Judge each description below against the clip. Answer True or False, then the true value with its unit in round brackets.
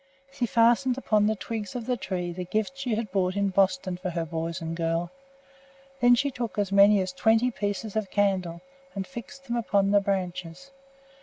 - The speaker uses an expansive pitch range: False (4.0 semitones)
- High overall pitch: True (200 Hz)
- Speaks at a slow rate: False (190 wpm)